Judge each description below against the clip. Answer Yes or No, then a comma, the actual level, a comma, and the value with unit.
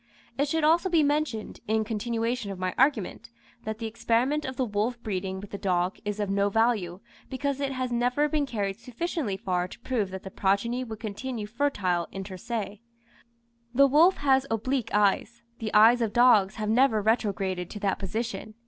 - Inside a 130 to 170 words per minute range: No, average, 185 wpm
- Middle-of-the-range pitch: No, high, 225 Hz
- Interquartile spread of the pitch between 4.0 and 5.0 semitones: Yes, average, 4.3 semitones